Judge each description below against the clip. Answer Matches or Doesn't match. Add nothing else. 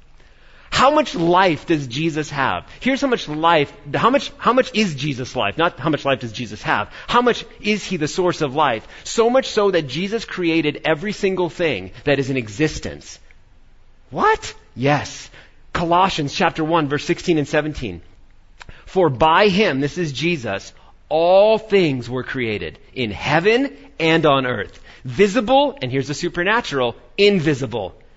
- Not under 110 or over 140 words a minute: Doesn't match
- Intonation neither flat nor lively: Doesn't match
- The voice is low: Doesn't match